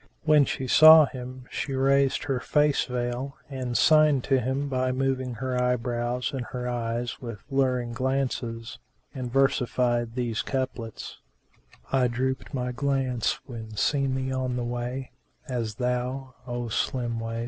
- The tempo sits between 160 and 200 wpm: No, average, 150 wpm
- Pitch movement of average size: No, narrow, 1.7 semitones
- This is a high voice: No, low, 125 Hz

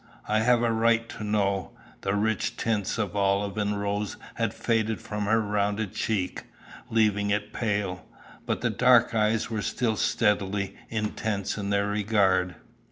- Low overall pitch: Yes, low, 105 Hz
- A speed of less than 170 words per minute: Yes, average, 155 wpm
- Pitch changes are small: Yes, narrow, 1.7 semitones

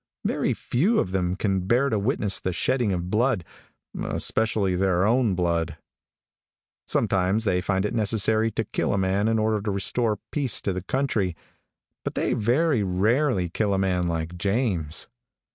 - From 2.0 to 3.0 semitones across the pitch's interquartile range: No, average, 3.6 semitones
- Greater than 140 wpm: Yes, average, 160 wpm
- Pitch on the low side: Yes, low, 100 Hz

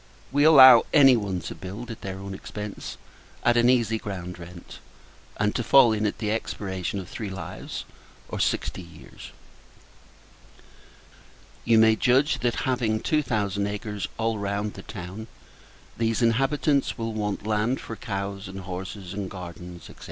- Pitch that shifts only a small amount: No, average, 3.3 semitones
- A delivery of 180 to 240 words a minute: No, average, 155 wpm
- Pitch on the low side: Yes, low, 105 Hz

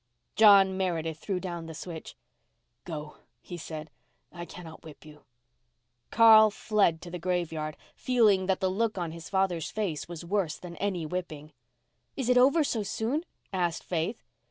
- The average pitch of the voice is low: No, medium, 180 Hz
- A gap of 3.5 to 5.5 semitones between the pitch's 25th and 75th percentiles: Yes, average, 3.9 semitones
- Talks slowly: No, average, 155 wpm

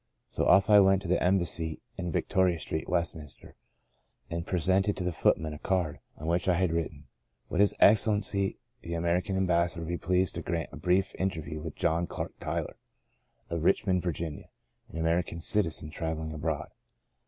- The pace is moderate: Yes, average, 185 wpm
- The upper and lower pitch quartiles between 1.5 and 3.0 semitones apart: Yes, narrow, 2.5 semitones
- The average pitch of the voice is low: Yes, very low, 85 Hz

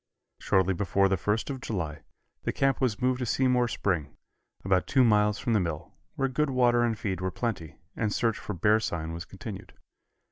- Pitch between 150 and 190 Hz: No, low, 105 Hz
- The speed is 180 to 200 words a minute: Yes, average, 190 wpm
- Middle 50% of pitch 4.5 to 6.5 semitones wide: Yes, average, 4.8 semitones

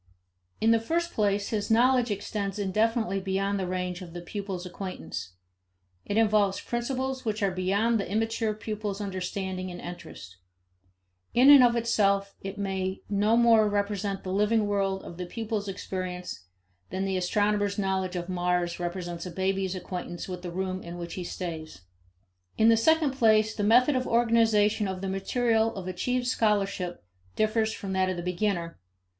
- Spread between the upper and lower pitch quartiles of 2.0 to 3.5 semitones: Yes, average, 3.1 semitones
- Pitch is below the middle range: No, high, 200 Hz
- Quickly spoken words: No, average, 165 wpm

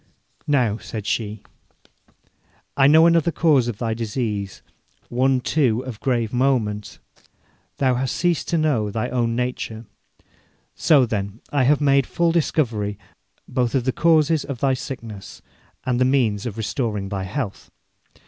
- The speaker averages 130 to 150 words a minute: Yes, average, 145 wpm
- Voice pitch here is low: Yes, low, 125 Hz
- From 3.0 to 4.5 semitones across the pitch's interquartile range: Yes, average, 4.1 semitones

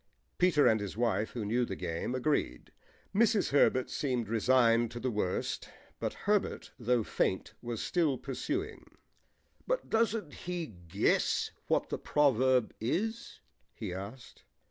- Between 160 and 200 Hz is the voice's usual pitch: No, low, 125 Hz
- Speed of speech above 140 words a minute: No, slow, 135 wpm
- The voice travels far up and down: Yes, wide, 7.4 semitones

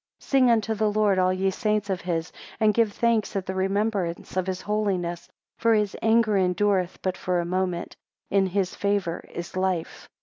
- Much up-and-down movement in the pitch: No, narrow, 2.6 semitones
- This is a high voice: Yes, high, 195 Hz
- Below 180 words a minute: No, average, 190 wpm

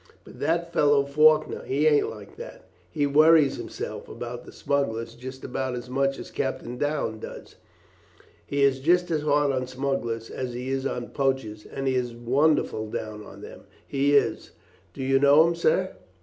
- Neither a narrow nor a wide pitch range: Yes, average, 3.0 semitones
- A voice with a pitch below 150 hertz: Yes, low, 135 Hz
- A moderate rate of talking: Yes, average, 175 wpm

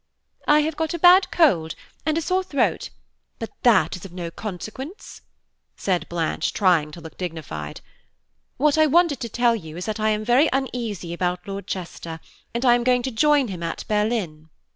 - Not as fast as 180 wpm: No, average, 185 wpm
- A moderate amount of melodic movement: No, wide, 7.8 semitones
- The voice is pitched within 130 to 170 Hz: No, high, 215 Hz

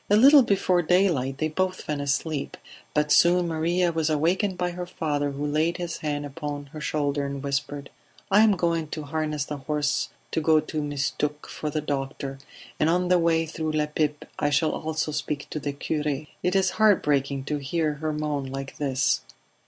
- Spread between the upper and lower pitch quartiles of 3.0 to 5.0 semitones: No, narrow, 2.6 semitones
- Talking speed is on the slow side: No, average, 190 wpm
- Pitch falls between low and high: Yes, medium, 150 Hz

